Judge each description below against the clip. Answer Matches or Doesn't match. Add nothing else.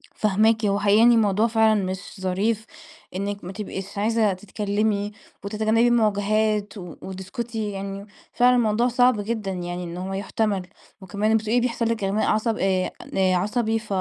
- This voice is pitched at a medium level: Doesn't match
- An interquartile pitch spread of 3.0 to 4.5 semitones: Doesn't match